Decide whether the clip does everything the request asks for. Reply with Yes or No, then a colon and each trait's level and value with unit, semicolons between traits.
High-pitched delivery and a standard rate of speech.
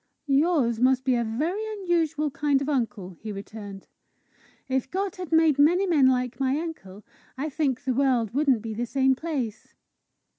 Yes: very high, 270 Hz; average, 170 wpm